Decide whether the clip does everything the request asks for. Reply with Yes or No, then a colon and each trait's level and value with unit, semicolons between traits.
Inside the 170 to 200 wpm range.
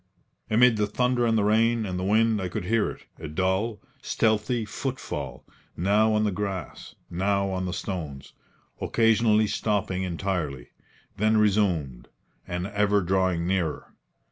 No: average, 145 wpm